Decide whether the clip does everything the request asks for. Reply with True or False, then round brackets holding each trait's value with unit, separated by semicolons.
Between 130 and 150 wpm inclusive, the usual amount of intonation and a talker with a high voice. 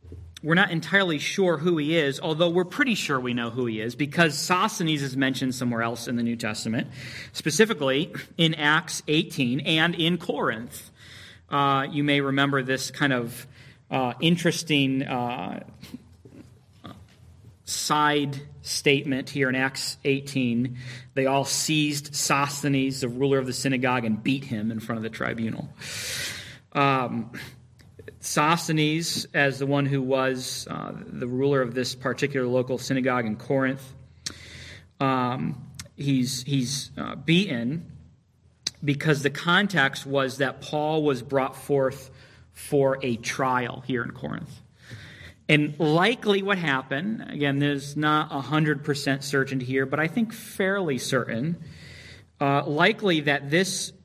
False (135 wpm; 3.0 semitones; 140 Hz)